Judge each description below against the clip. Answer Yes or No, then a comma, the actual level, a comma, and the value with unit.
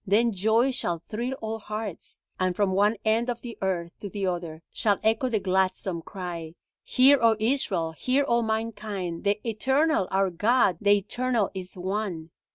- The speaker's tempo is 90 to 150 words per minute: No, average, 165 wpm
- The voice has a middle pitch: No, high, 205 Hz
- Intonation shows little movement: No, average, 3.7 semitones